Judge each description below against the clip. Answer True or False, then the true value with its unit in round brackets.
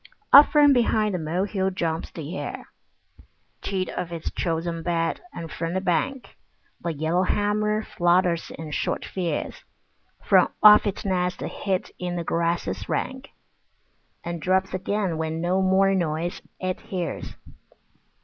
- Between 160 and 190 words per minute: False (135 wpm)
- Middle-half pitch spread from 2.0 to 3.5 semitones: True (2.6 semitones)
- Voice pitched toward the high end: False (180 Hz)